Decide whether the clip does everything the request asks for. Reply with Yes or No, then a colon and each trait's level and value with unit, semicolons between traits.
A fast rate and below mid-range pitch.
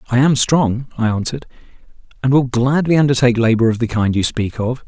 No: average, 195 wpm; low, 125 Hz